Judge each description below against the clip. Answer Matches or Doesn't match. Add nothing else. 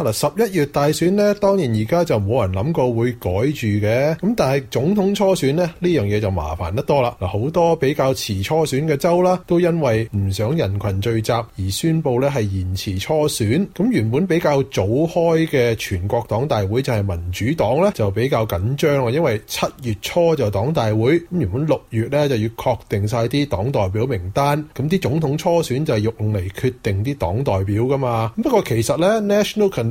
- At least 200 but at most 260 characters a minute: Doesn't match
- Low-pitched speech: Matches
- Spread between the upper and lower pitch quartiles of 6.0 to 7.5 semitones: Matches